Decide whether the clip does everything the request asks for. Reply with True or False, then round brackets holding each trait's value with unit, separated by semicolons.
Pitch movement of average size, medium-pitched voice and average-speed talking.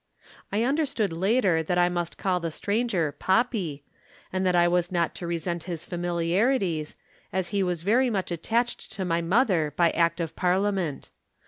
True (3.3 semitones; 180 Hz; 165 wpm)